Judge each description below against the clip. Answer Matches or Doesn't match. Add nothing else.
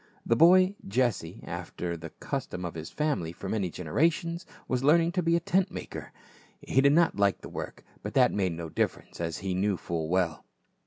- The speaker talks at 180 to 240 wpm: Matches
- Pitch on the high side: Doesn't match